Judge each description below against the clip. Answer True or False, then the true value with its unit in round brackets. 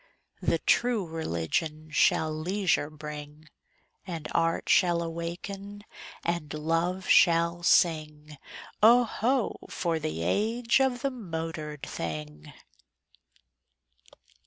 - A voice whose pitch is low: False (165 Hz)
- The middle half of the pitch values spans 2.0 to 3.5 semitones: False (4.4 semitones)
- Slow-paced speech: True (95 wpm)